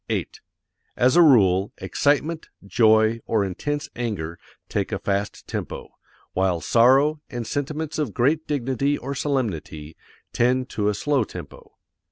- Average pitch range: No, wide, 6.1 semitones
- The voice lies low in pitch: Yes, low, 120 Hz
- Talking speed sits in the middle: No, slow, 130 wpm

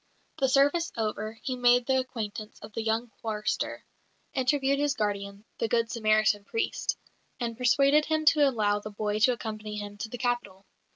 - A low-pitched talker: No, high, 230 Hz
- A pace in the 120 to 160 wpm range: No, average, 170 wpm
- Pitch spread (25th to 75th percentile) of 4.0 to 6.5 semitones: No, average, 3.6 semitones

